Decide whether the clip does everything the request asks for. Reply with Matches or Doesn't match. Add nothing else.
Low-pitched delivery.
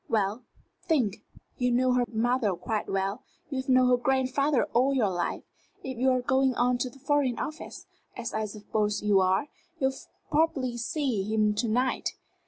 Doesn't match